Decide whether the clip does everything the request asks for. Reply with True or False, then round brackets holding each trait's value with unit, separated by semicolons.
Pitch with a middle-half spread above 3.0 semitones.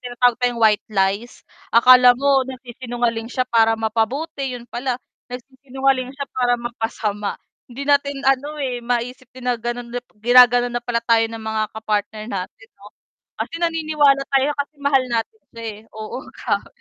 False (2.7 semitones)